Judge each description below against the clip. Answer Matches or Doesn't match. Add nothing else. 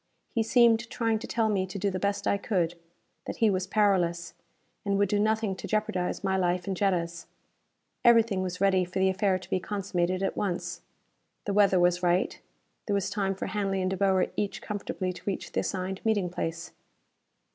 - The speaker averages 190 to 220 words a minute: Matches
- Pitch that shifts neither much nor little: Doesn't match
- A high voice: Matches